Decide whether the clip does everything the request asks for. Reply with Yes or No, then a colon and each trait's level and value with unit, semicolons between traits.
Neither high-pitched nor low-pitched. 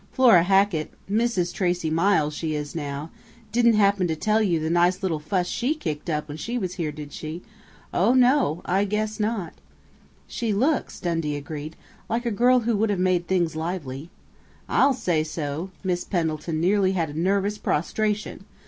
Yes: medium, 180 Hz